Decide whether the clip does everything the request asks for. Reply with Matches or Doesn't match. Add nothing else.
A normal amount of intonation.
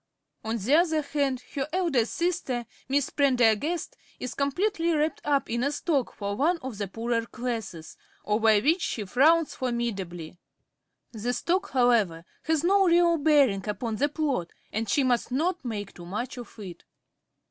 Doesn't match